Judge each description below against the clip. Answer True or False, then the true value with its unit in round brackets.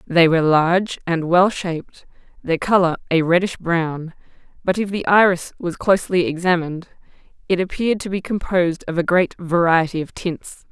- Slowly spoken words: False (160 wpm)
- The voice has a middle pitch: True (175 Hz)